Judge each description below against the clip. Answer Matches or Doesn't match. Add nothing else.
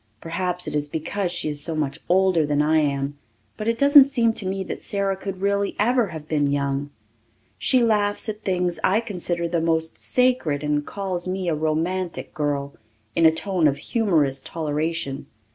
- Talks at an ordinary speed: Matches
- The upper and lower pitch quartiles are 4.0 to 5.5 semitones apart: Matches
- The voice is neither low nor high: Matches